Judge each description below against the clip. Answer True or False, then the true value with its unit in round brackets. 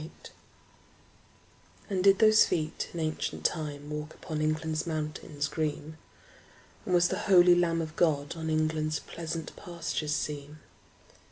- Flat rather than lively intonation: True (2.0 semitones)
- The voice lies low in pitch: False (155 Hz)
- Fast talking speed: False (145 wpm)